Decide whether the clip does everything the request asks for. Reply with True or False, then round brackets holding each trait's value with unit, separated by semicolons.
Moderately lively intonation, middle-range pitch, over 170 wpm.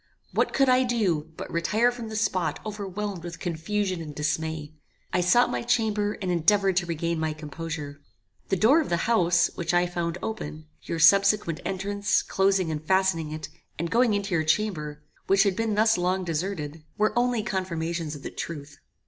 True (4.4 semitones; 180 Hz; 180 wpm)